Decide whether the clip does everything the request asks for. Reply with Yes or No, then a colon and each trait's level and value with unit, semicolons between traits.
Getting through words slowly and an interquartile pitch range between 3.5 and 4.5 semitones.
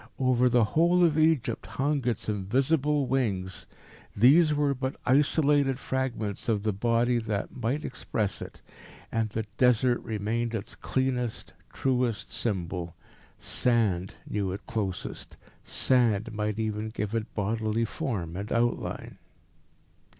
Yes: slow, 125 wpm; average, 3.8 semitones